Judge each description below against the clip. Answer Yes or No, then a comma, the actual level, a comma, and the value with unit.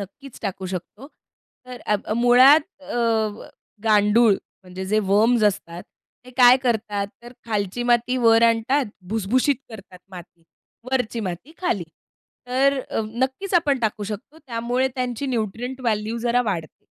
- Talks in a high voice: Yes, high, 235 Hz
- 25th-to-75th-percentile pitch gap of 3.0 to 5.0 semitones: Yes, average, 3.7 semitones